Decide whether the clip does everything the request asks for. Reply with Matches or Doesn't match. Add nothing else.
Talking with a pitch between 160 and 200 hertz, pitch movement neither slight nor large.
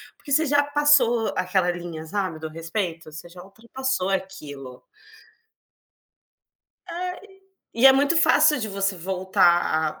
Doesn't match